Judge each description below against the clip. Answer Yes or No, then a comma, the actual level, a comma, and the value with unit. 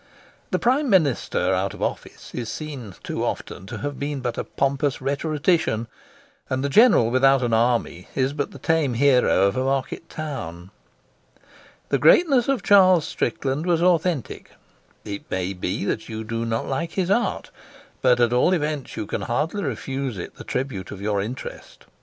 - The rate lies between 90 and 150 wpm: No, average, 170 wpm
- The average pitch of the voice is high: No, low, 135 Hz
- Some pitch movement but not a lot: No, wide, 5.8 semitones